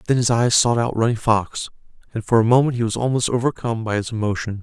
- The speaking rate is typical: No, fast, 235 wpm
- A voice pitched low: Yes, low, 115 Hz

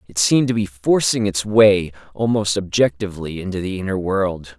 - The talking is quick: No, average, 170 wpm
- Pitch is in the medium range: No, low, 100 Hz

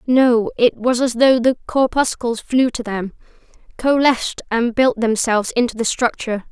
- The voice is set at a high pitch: Yes, high, 240 Hz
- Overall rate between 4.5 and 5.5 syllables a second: Yes, 4.9 syllables/s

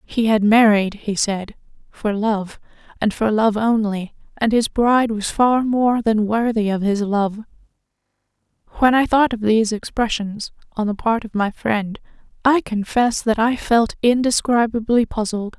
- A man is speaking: No, female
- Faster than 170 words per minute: No, average, 160 wpm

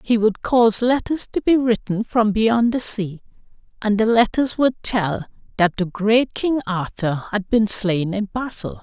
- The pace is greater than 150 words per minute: Yes, average, 175 wpm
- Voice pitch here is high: Yes, high, 215 Hz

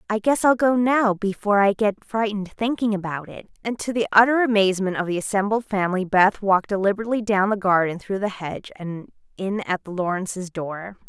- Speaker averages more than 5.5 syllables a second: Yes, 5.9 syllables/s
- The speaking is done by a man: No, female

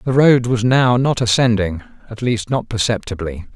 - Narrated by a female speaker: No, male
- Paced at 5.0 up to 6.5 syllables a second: No, 4.8 syllables/s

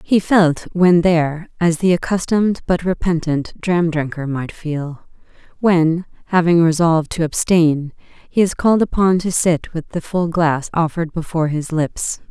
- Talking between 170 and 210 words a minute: No, average, 155 wpm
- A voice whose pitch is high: No, medium, 165 Hz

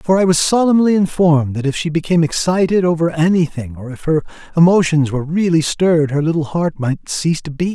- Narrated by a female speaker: No, male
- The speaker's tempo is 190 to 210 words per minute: Yes, average, 200 wpm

